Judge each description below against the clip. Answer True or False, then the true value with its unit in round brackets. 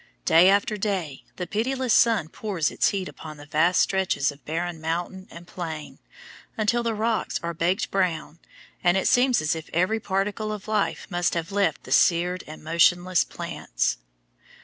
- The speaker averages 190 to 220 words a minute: False (170 wpm)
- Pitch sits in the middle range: True (180 Hz)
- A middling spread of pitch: True (4.0 semitones)